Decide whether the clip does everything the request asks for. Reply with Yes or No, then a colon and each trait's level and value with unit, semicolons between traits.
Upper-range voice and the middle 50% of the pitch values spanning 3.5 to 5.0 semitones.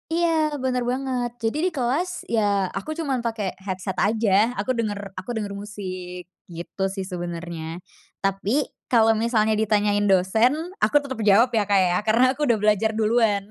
Yes: high, 215 Hz; average, 3.8 semitones